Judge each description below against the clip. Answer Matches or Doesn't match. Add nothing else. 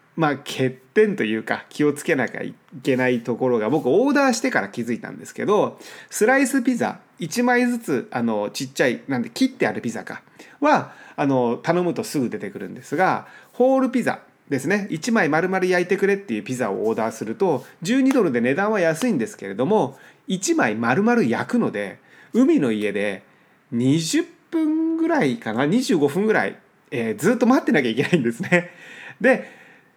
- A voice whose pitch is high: Matches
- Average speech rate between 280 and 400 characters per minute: Matches